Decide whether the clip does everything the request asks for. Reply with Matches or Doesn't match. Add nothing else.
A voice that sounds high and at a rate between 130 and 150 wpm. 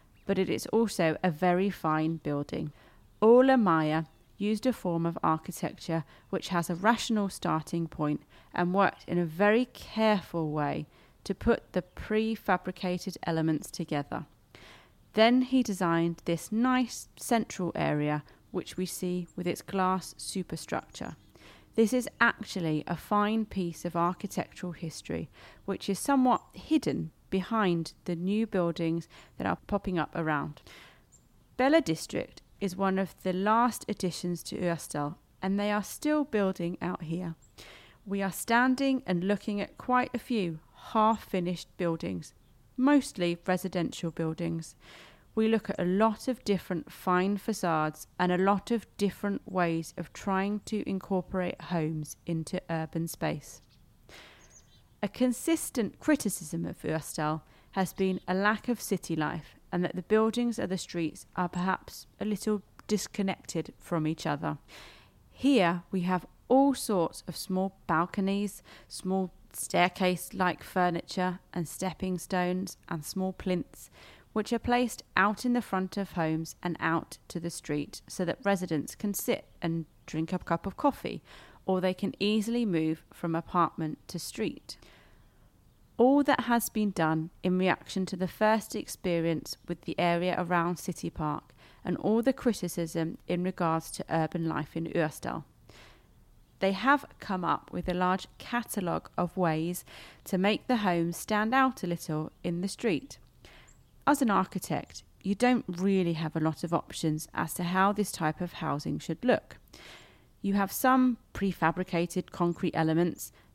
Doesn't match